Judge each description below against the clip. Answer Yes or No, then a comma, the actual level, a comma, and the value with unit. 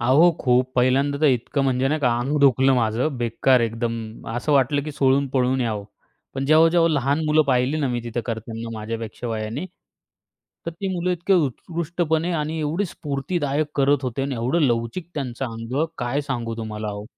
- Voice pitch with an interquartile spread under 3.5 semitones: No, average, 4.3 semitones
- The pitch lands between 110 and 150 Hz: Yes, low, 135 Hz